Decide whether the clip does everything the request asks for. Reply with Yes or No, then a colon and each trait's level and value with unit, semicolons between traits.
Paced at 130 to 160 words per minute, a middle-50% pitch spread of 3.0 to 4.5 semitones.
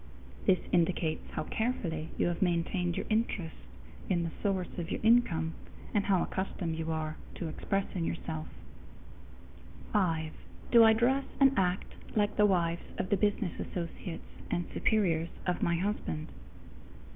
Yes: average, 145 wpm; average, 3.8 semitones